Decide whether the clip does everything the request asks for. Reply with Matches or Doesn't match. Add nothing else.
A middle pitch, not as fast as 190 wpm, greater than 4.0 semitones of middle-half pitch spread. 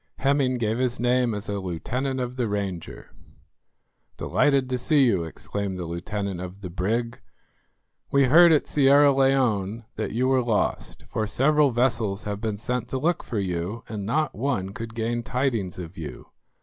Doesn't match